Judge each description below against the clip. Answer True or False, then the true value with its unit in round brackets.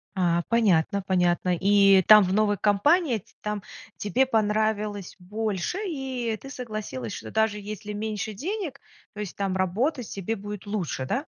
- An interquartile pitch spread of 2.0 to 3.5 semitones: True (2.9 semitones)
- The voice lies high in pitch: True (210 Hz)